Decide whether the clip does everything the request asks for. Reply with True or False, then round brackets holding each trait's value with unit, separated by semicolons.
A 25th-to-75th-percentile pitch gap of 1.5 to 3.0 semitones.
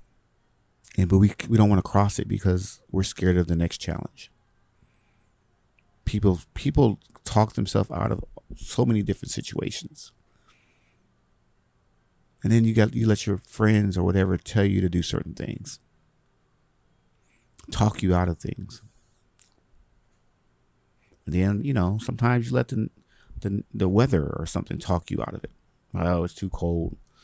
False (3.7 semitones)